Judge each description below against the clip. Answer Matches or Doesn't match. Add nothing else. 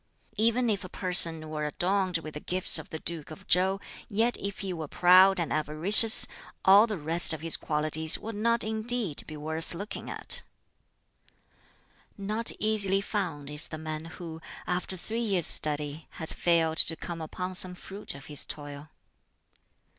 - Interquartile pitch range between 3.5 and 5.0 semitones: Matches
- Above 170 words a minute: Doesn't match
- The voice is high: Doesn't match